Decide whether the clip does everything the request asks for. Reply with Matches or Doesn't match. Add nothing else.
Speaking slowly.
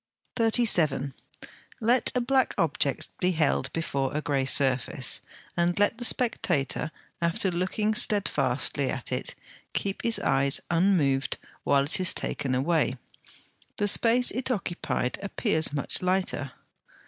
Matches